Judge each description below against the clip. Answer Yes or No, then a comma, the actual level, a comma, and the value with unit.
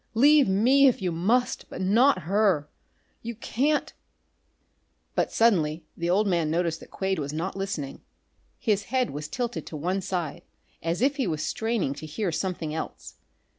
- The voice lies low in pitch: No, high, 190 Hz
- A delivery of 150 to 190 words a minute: Yes, average, 170 wpm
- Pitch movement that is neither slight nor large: No, wide, 6.1 semitones